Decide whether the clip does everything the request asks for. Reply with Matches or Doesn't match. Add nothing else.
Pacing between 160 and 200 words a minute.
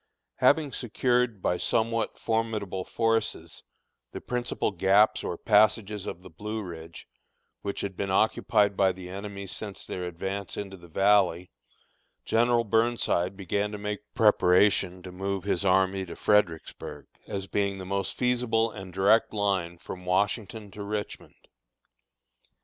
Doesn't match